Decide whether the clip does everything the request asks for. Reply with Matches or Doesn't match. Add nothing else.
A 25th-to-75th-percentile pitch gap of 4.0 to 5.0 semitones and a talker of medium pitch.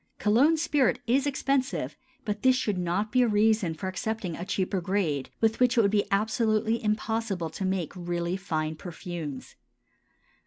Doesn't match